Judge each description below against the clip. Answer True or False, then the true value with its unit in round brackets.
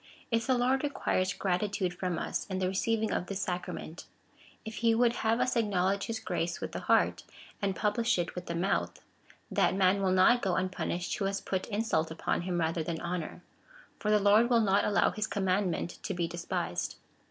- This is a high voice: True (195 Hz)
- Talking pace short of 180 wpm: False (200 wpm)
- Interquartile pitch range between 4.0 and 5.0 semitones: False (3.6 semitones)